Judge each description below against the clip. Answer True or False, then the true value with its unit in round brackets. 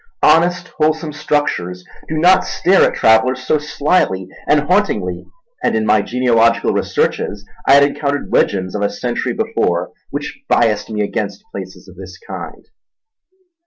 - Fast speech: False (145 wpm)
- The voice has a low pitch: True (130 Hz)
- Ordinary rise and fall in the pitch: False (6.8 semitones)